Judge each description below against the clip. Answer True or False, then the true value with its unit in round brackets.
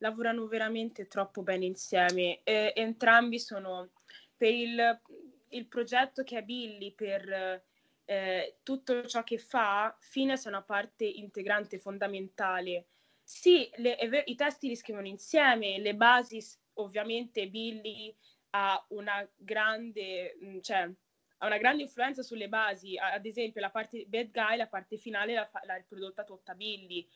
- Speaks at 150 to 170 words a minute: False (135 wpm)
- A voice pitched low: False (215 Hz)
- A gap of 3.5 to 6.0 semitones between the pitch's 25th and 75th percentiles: False (3.0 semitones)